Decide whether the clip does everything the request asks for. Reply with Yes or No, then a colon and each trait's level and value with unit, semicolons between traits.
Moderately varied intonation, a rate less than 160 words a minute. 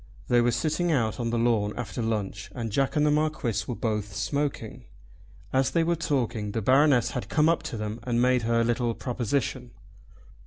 No: average, 3.4 semitones; average, 190 wpm